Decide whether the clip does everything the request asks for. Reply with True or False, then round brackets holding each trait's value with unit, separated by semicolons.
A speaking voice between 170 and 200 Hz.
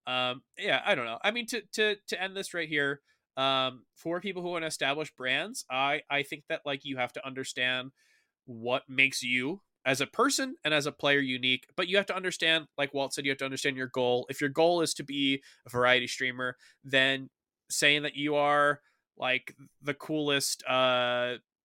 False (140 Hz)